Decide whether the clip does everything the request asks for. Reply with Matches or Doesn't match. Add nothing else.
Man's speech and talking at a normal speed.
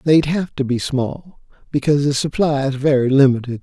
Matches